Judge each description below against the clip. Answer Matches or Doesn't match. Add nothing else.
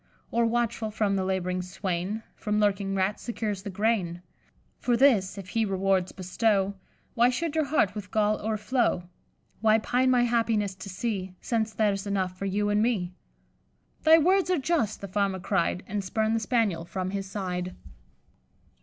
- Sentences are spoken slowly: Doesn't match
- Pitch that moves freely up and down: Doesn't match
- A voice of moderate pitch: Doesn't match